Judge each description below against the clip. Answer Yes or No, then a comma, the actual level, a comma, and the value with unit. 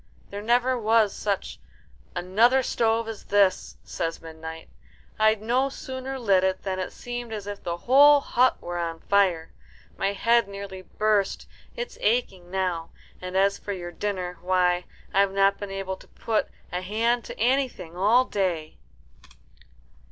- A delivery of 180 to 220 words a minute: No, average, 150 wpm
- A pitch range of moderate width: Yes, average, 4.0 semitones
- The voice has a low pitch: No, high, 200 Hz